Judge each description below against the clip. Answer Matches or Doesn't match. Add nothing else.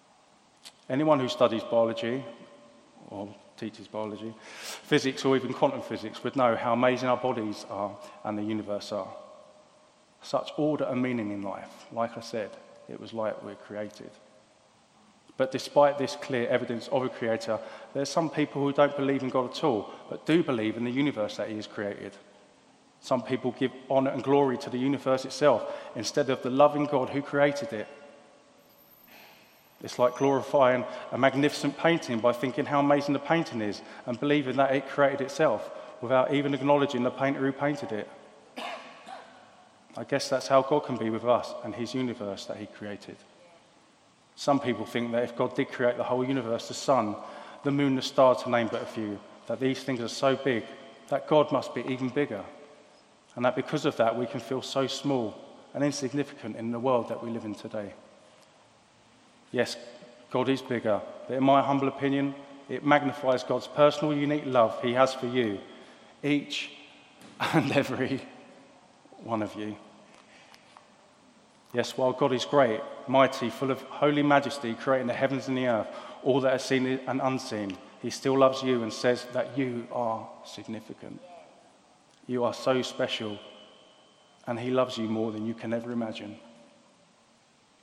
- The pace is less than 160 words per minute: Doesn't match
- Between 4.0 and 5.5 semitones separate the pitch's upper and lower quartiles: Doesn't match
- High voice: Doesn't match